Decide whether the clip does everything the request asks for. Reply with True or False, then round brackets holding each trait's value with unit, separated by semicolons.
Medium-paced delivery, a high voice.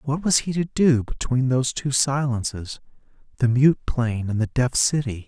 False (170 wpm; 130 Hz)